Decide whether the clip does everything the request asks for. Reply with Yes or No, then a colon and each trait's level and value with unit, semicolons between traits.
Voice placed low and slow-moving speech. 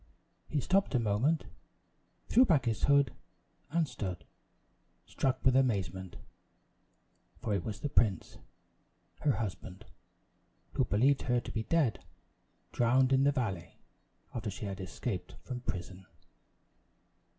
Yes: low, 120 Hz; slow, 125 wpm